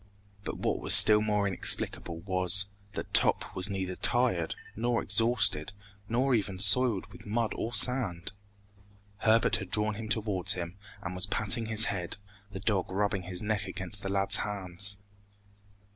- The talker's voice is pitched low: Yes, low, 100 Hz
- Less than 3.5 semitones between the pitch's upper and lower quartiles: Yes, average, 2.7 semitones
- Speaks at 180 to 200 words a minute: No, average, 155 wpm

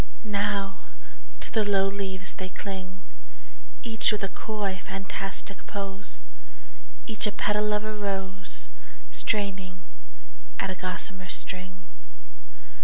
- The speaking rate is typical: No, slow, 110 wpm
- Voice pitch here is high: Yes, high, 195 Hz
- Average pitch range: No, narrow, 1.6 semitones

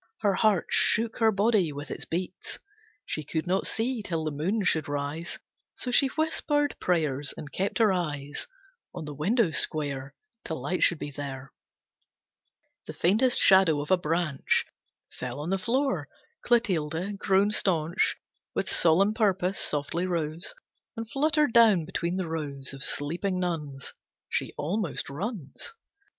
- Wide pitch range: Yes, wide, 5.7 semitones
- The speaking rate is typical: Yes, average, 145 wpm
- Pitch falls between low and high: Yes, medium, 175 Hz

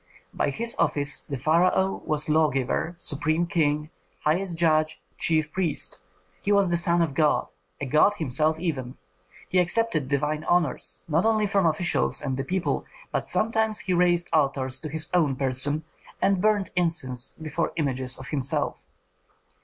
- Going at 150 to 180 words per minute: Yes, average, 155 wpm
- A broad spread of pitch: No, average, 3.7 semitones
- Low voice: No, medium, 155 Hz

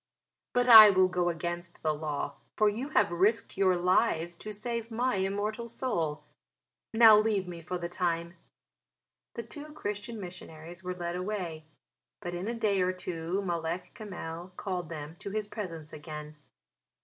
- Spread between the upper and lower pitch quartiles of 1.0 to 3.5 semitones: No, average, 3.9 semitones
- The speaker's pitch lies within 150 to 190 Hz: Yes, medium, 185 Hz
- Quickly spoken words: No, average, 160 wpm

